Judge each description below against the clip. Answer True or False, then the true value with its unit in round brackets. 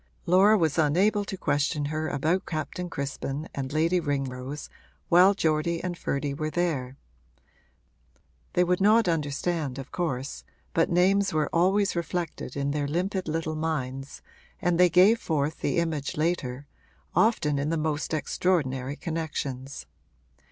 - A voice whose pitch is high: False (160 Hz)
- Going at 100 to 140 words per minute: True (135 wpm)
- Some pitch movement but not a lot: True (3.8 semitones)